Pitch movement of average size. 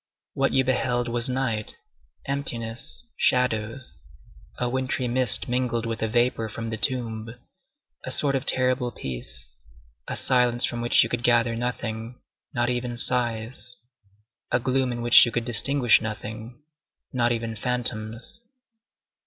No: narrow, 1.8 semitones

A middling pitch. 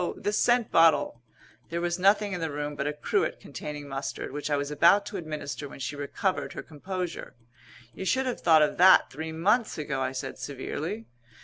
Yes: medium, 160 Hz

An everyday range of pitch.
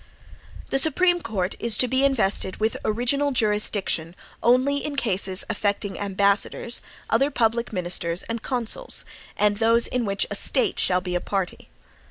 Yes: average, 4.7 semitones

